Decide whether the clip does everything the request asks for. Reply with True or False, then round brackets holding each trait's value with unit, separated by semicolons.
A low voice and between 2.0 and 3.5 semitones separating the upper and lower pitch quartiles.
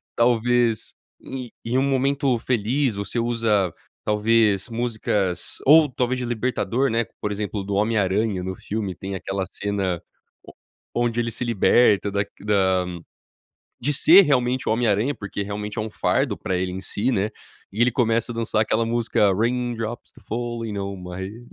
True (110 Hz; 3.1 semitones)